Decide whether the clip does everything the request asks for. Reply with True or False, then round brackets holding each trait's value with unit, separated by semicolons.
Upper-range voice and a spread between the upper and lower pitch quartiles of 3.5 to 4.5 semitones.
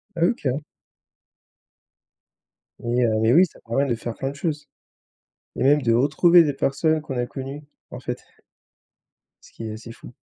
False (135 Hz; 4.1 semitones)